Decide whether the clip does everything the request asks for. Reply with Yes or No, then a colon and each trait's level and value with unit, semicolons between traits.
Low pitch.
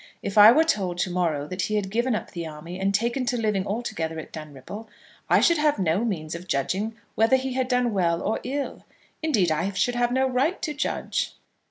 No: high, 210 Hz